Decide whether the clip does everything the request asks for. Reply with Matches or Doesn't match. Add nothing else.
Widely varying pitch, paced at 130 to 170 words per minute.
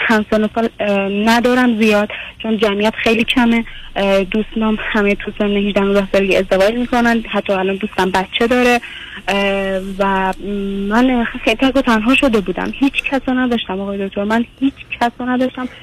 Doesn't match